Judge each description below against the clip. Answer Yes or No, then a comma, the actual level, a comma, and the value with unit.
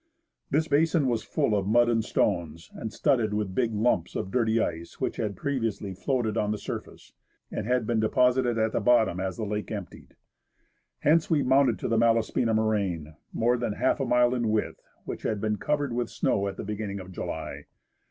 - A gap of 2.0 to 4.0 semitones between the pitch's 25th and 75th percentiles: Yes, average, 3.1 semitones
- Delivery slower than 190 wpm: No, average, 195 wpm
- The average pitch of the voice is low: Yes, low, 110 Hz